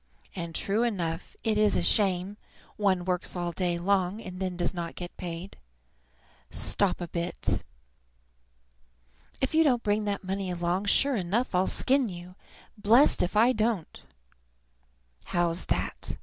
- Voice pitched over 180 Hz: Yes, high, 190 Hz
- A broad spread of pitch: No, average, 3.3 semitones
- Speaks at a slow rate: No, average, 145 wpm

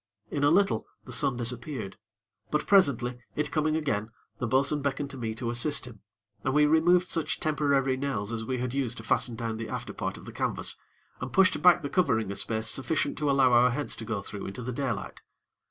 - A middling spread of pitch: Yes, average, 4.3 semitones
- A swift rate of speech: Yes, fast, 215 wpm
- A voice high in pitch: No, low, 130 Hz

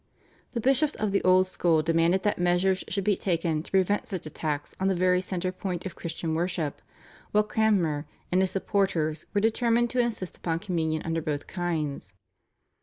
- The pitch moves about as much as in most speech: Yes, average, 3.3 semitones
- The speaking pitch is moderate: Yes, medium, 180 Hz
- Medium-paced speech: Yes, average, 180 wpm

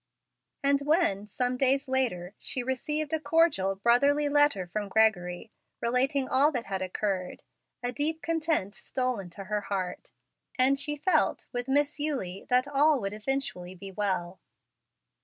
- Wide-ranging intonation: Yes, wide, 6.4 semitones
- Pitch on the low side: No, very high, 250 Hz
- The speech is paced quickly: No, average, 145 wpm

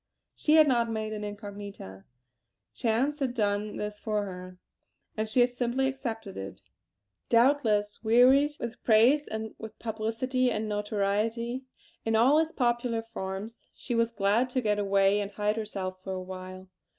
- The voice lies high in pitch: Yes, high, 220 Hz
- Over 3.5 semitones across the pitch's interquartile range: No, average, 3.0 semitones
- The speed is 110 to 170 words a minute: Yes, average, 155 wpm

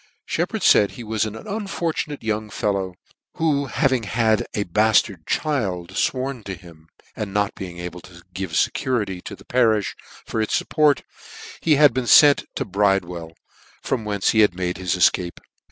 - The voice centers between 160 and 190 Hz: No, low, 105 Hz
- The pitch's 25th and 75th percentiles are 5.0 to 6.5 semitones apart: Yes, wide, 5.6 semitones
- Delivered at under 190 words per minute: Yes, average, 165 wpm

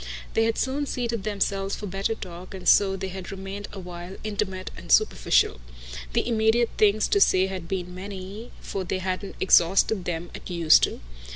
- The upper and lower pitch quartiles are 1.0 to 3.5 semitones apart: Yes, narrow, 2.5 semitones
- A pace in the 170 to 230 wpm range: Yes, average, 175 wpm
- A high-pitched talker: Yes, high, 195 Hz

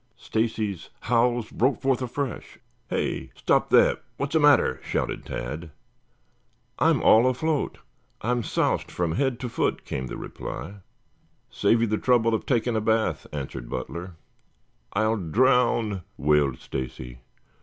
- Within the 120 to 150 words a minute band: Yes, slow, 135 wpm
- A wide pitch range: Yes, wide, 6.4 semitones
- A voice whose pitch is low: Yes, low, 110 Hz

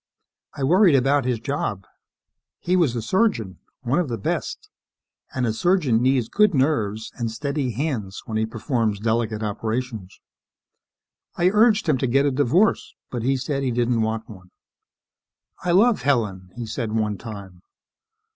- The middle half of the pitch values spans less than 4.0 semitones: No, average, 4.6 semitones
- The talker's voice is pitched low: Yes, low, 125 Hz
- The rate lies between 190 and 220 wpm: No, average, 155 wpm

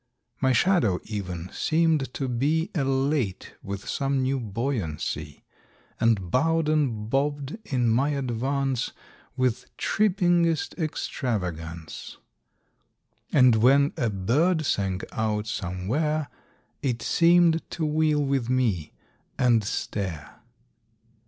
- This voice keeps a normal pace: No, slow, 100 wpm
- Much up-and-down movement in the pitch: Yes, wide, 6.0 semitones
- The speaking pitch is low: Yes, low, 130 Hz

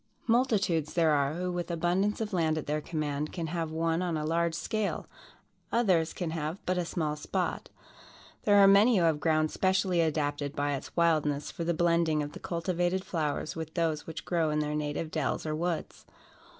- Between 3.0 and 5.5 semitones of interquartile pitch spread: No, narrow, 2.6 semitones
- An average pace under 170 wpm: No, average, 190 wpm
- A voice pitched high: No, medium, 165 Hz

